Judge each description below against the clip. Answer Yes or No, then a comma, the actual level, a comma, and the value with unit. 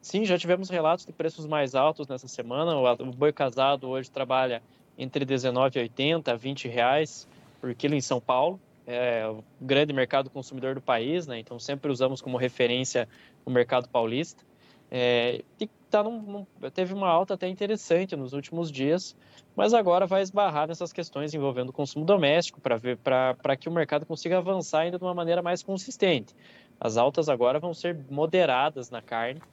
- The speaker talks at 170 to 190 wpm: Yes, average, 175 wpm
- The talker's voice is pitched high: No, medium, 145 Hz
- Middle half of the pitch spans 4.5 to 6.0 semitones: Yes, average, 5.2 semitones